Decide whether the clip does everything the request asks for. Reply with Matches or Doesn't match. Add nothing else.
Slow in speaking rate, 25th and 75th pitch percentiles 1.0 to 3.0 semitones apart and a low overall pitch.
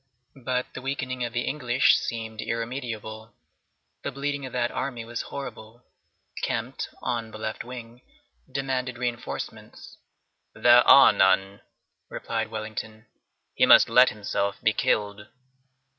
Matches